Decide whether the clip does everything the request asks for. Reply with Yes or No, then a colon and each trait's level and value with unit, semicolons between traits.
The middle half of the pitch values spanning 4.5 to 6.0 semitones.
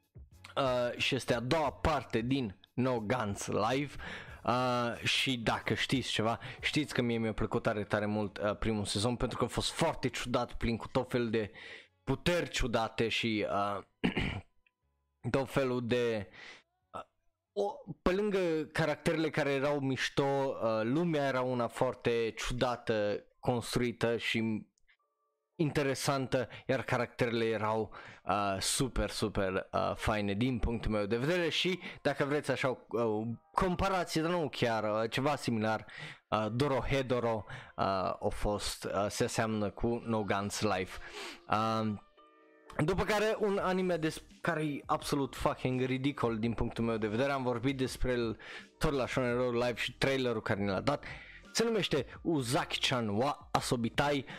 No: average, 4.1 semitones